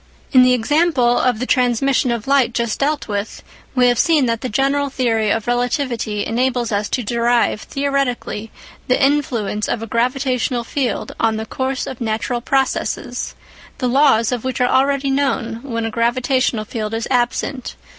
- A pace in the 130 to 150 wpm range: No, average, 165 wpm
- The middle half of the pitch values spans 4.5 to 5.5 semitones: No, average, 2.8 semitones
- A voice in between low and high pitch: No, high, 245 Hz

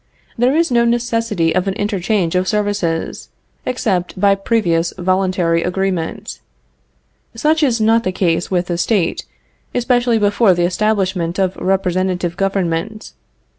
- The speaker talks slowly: Yes, slow, 130 wpm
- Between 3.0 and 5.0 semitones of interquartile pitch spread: Yes, average, 4.0 semitones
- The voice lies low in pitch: No, high, 195 Hz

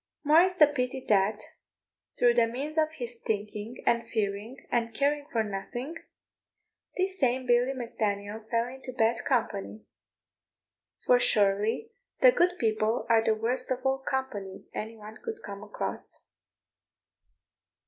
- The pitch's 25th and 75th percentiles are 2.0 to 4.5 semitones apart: Yes, average, 3.6 semitones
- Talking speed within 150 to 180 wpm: No, average, 140 wpm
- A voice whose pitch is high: Yes, high, 235 Hz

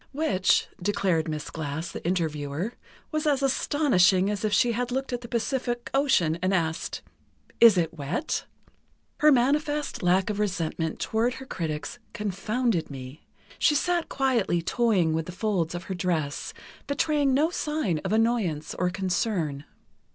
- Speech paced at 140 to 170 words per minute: Yes, average, 150 wpm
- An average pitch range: No, wide, 7.2 semitones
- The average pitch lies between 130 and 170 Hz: No, high, 200 Hz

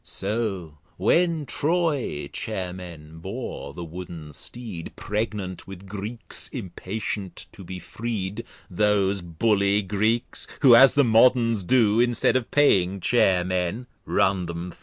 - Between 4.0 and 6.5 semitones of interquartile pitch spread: Yes, average, 4.5 semitones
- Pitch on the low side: Yes, low, 100 Hz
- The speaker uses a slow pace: Yes, slow, 130 wpm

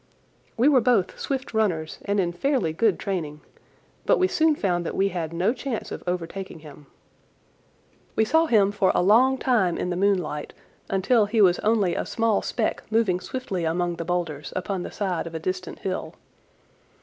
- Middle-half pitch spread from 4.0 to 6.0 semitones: Yes, average, 4.5 semitones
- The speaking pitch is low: No, high, 190 Hz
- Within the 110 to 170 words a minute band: No, average, 180 wpm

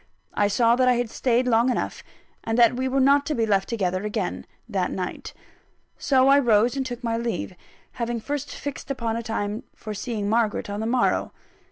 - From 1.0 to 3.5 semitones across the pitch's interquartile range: Yes, average, 3.2 semitones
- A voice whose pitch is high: Yes, high, 235 Hz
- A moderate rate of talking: Yes, average, 195 wpm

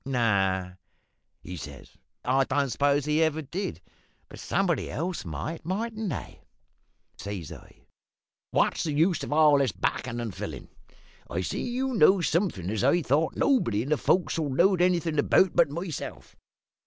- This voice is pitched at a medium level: Yes, medium, 150 Hz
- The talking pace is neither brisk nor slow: Yes, average, 155 wpm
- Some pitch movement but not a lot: No, wide, 6.8 semitones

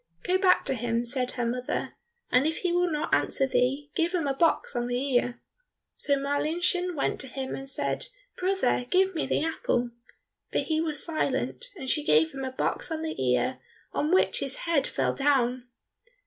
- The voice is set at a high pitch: Yes, very high, 280 Hz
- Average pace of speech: Yes, average, 190 wpm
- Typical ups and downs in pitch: Yes, average, 4.7 semitones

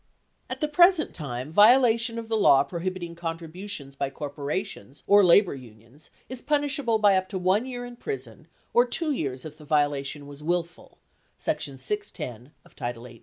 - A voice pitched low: No, medium, 170 Hz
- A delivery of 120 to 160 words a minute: No, average, 170 wpm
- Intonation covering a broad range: Yes, wide, 8.5 semitones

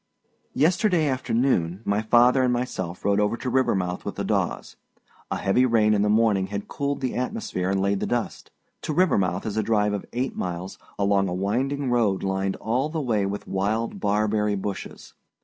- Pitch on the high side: No, low, 105 Hz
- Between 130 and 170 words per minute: No, average, 185 wpm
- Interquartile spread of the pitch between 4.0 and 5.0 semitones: Yes, average, 4.4 semitones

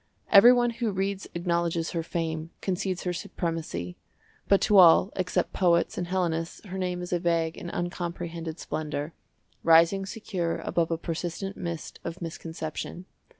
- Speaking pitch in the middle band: Yes, medium, 170 Hz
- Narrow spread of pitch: Yes, narrow, 2.2 semitones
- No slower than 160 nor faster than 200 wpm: No, average, 150 wpm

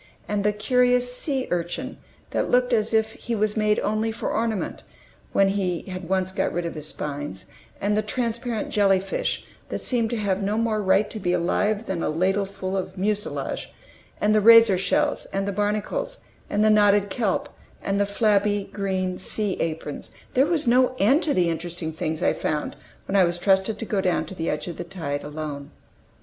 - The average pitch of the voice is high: Yes, high, 200 Hz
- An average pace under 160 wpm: No, average, 195 wpm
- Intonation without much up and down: No, average, 3.3 semitones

